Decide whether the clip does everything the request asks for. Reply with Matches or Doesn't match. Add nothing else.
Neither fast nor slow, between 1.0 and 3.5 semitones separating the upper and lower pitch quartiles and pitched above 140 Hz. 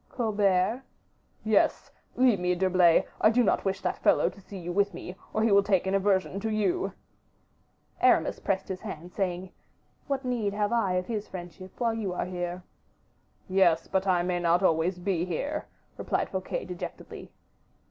Matches